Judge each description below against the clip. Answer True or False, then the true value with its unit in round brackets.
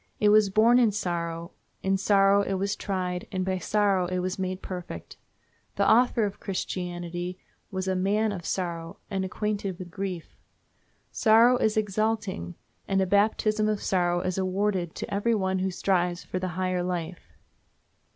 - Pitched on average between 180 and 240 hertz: True (190 Hz)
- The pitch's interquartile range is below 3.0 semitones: True (2.4 semitones)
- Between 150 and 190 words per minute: True (160 wpm)